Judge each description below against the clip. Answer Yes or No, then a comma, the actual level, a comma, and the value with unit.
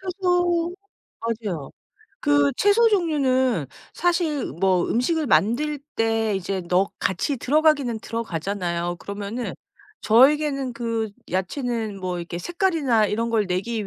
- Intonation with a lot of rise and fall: Yes, wide, 7.6 semitones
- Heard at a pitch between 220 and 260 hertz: Yes, high, 230 Hz